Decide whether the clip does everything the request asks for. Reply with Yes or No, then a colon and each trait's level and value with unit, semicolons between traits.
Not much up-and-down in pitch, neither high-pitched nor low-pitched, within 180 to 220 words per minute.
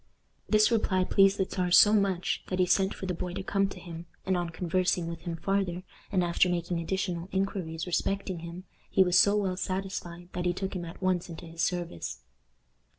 Yes: narrow, 2.0 semitones; medium, 180 Hz; fast, 205 wpm